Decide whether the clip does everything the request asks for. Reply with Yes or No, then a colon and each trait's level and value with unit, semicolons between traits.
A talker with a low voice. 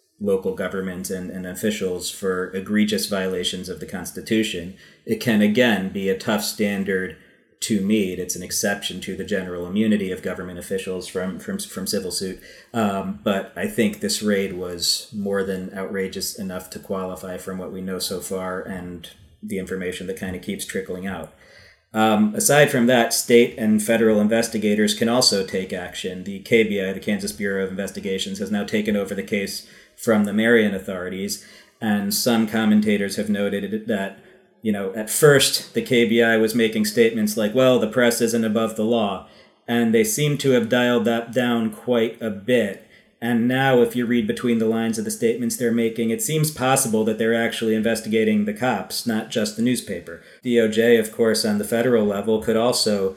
Yes: low, 110 Hz